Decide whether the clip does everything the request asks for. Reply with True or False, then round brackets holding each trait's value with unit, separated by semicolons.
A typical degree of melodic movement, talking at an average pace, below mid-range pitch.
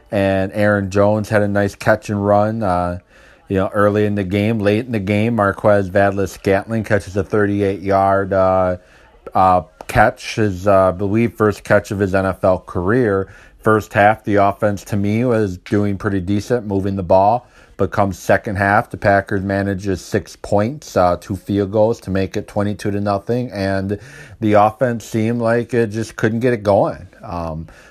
False (1.7 semitones; 180 wpm; 100 Hz)